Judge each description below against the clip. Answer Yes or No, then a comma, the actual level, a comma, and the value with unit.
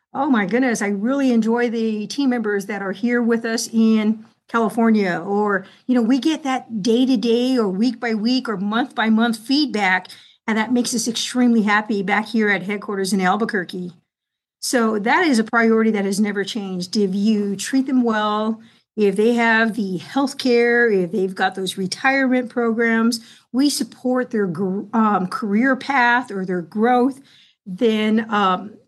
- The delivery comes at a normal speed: Yes, average, 170 wpm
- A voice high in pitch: Yes, high, 225 Hz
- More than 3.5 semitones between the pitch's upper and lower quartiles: No, average, 2.9 semitones